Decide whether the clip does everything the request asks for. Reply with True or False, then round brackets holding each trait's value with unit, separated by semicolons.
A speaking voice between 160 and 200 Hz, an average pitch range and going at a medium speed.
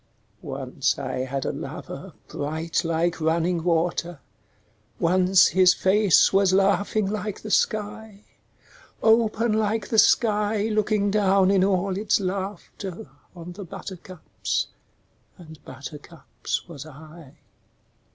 False (190 Hz; 3.7 semitones; 110 wpm)